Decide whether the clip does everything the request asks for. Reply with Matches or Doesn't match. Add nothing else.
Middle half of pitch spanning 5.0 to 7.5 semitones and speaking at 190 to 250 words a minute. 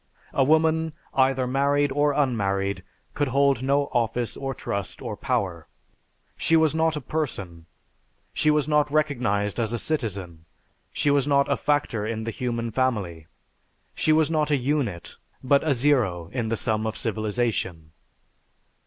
Doesn't match